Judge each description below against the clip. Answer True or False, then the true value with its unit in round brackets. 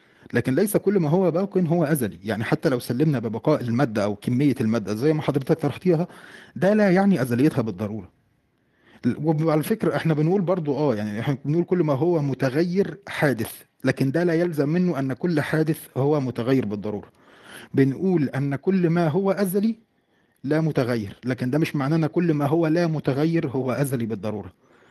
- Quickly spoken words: True (175 wpm)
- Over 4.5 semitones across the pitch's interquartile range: True (5.0 semitones)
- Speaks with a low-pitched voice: False (150 Hz)